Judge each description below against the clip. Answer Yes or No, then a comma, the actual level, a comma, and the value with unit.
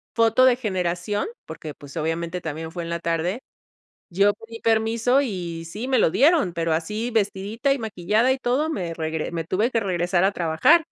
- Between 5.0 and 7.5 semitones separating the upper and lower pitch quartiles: Yes, wide, 5.4 semitones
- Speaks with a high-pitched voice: Yes, high, 195 Hz